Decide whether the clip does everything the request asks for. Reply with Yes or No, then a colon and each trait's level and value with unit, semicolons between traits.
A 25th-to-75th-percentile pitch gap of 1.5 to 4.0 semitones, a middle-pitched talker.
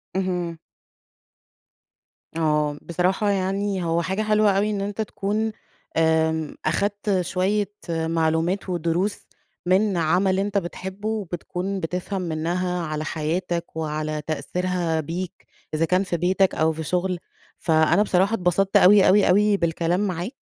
Yes: average, 3.2 semitones; medium, 180 Hz